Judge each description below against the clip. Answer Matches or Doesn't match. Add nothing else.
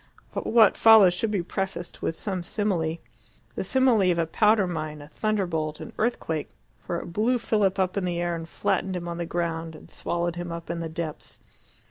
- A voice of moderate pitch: Matches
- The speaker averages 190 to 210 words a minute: Matches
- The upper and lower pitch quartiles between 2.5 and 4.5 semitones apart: Matches